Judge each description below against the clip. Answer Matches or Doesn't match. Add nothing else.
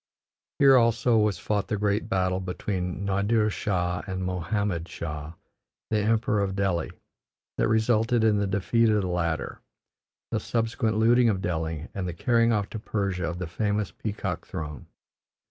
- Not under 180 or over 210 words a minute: Doesn't match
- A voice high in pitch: Doesn't match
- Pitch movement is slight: Doesn't match